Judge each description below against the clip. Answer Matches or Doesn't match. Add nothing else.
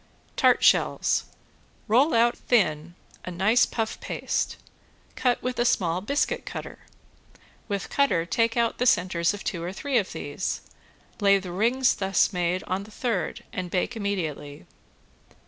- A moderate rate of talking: Matches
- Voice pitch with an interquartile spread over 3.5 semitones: Matches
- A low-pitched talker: Doesn't match